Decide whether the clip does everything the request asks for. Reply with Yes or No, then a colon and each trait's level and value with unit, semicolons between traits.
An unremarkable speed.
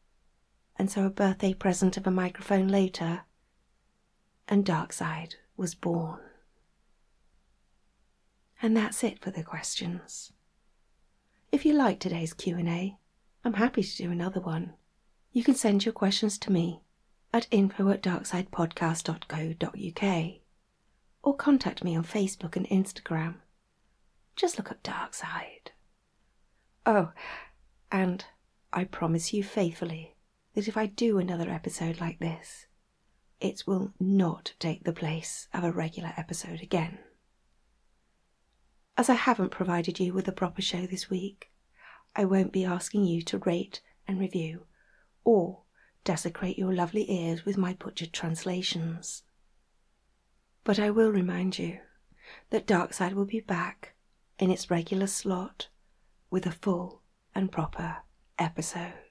No: slow, 130 wpm